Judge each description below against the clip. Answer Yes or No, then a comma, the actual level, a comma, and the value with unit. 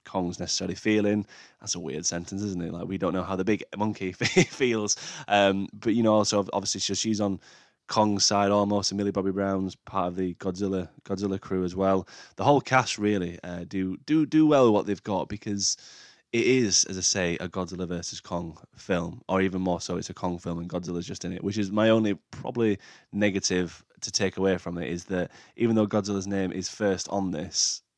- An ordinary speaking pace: No, fast, 210 wpm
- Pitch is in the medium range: No, very low, 95 Hz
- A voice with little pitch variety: Yes, narrow, 2.3 semitones